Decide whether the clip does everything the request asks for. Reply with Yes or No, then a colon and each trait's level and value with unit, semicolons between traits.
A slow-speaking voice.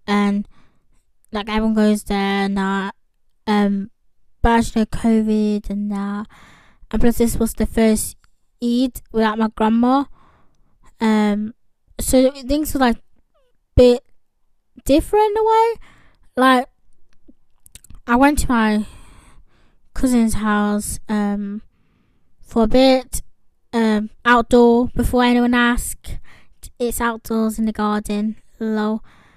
Yes: slow, 115 wpm